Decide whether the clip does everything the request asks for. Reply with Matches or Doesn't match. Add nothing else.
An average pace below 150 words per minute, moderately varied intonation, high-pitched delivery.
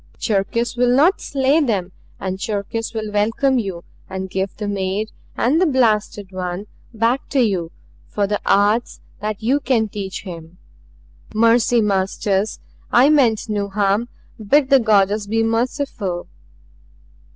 Matches